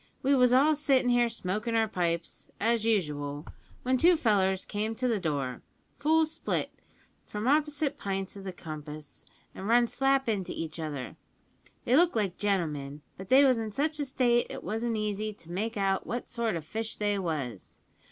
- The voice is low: No, high, 215 Hz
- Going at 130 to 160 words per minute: No, average, 180 wpm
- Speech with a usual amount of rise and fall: No, wide, 5.7 semitones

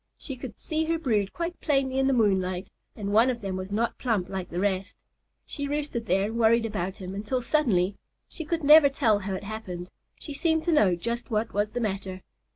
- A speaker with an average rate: No, fast, 215 wpm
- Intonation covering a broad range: Yes, wide, 5.9 semitones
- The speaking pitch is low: No, high, 220 Hz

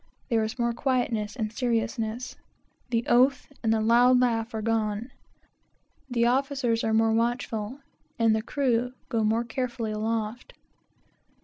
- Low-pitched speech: No, high, 230 Hz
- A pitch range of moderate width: No, narrow, 1.9 semitones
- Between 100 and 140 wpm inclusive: Yes, slow, 135 wpm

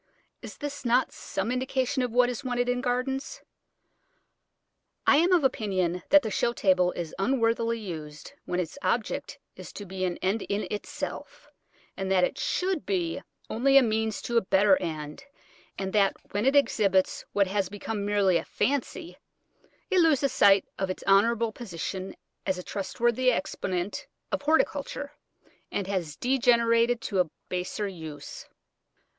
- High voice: Yes, high, 215 Hz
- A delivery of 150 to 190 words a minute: Yes, average, 155 wpm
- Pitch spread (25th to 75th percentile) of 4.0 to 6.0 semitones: Yes, average, 4.9 semitones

